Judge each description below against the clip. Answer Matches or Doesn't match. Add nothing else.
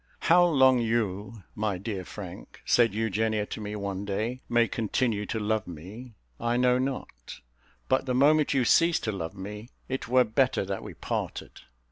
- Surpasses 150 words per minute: Matches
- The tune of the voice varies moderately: Matches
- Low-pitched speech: Matches